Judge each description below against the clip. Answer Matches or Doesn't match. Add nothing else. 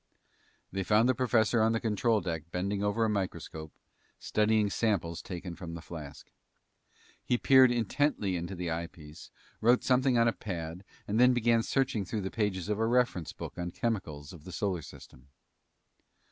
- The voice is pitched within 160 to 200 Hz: Doesn't match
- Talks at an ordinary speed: Matches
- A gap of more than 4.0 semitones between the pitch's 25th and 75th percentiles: Matches